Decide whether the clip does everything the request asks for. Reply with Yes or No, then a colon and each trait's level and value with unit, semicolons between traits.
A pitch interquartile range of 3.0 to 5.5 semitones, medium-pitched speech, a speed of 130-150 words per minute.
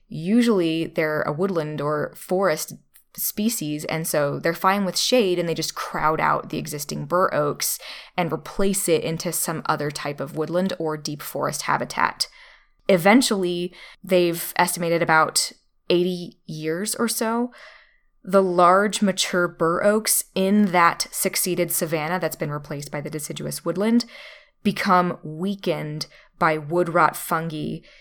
Yes: average, 3.4 semitones; medium, 175 Hz; average, 140 wpm